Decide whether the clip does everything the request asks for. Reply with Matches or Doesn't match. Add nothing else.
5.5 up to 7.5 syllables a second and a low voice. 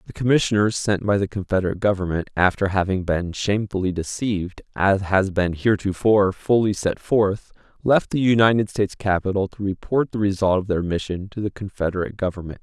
Matches